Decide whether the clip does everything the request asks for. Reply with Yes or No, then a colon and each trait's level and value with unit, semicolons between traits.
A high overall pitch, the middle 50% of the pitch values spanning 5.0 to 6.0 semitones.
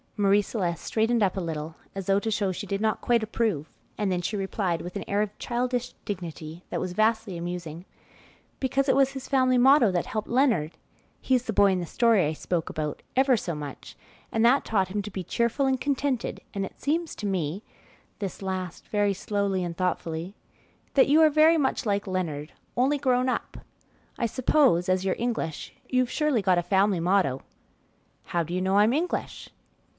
Yes: high, 205 Hz; wide, 5.5 semitones